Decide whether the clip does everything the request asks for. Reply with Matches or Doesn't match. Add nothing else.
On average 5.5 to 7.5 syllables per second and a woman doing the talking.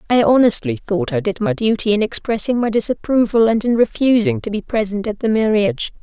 Matches